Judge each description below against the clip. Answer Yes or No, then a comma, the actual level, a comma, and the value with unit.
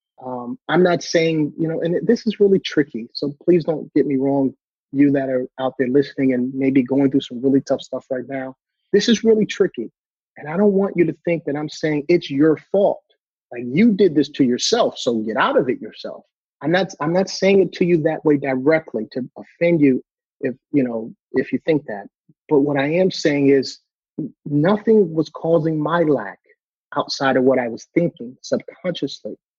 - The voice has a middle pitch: Yes, medium, 145 Hz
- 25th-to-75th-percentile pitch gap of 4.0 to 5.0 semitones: Yes, average, 4.5 semitones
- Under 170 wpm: No, fast, 205 wpm